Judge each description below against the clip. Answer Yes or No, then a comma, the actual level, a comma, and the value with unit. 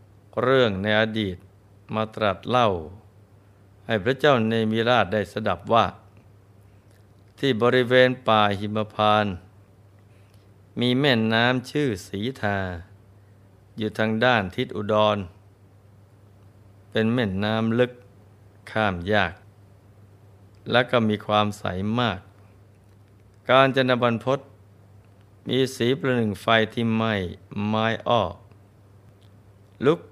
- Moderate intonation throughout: No, narrow, 2.1 semitones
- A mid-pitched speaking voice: No, low, 105 Hz